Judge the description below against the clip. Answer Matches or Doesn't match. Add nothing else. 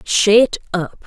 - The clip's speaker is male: Doesn't match